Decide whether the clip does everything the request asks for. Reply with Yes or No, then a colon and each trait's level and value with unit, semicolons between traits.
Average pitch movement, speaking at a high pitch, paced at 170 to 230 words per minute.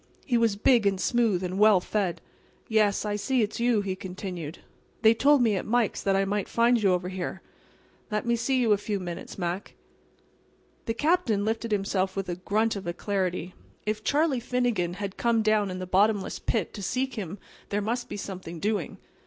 Yes: average, 3.5 semitones; high, 205 Hz; average, 195 wpm